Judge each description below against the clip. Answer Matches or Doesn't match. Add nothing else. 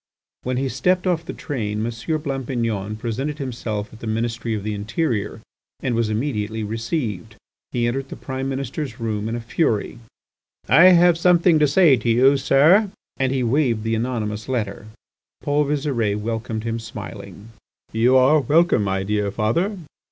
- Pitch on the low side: Matches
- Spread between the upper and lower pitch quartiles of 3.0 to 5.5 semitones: Matches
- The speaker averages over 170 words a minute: Doesn't match